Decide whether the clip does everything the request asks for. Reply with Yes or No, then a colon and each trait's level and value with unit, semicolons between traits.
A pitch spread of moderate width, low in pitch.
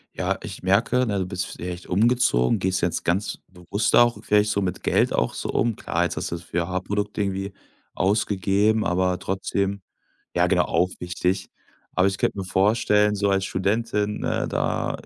No: narrow, 2.3 semitones; very low, 95 Hz